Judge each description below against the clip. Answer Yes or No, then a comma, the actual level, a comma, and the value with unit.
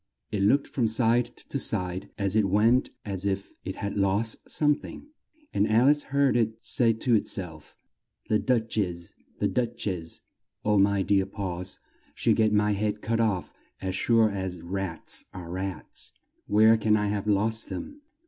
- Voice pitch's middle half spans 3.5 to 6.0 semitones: No, average, 2.9 semitones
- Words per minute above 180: No, average, 175 wpm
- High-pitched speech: No, low, 105 Hz